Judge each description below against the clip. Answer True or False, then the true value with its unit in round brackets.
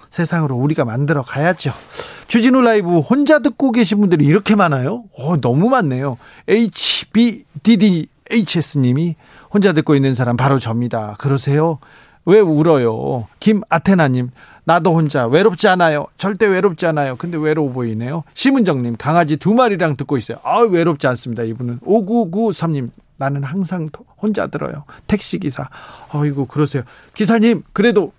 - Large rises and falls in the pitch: True (6.9 semitones)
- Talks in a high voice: False (165 Hz)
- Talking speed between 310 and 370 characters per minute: True (330 characters per minute)